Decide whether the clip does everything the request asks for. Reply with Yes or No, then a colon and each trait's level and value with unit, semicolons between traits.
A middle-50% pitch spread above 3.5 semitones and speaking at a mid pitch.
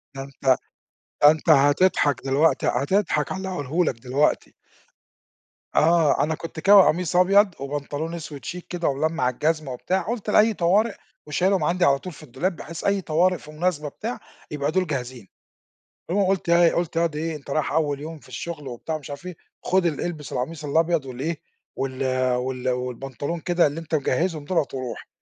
Yes: average, 4.0 semitones; medium, 155 Hz